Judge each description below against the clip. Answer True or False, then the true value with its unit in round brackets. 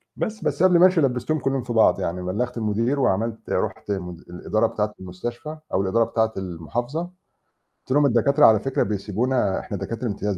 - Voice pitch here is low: True (115 Hz)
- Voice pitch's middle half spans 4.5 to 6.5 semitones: True (5.1 semitones)